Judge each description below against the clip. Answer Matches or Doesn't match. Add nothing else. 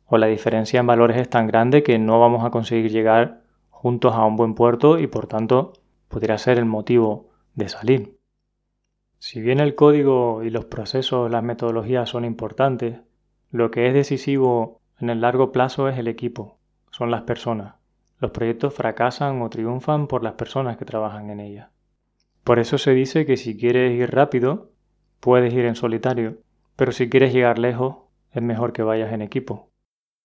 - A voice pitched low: Matches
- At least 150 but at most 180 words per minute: Matches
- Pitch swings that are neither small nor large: Doesn't match